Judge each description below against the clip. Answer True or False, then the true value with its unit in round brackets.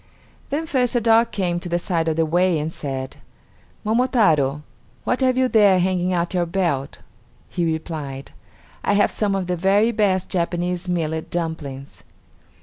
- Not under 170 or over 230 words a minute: False (160 wpm)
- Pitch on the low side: False (175 Hz)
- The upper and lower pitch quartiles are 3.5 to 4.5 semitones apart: True (4.2 semitones)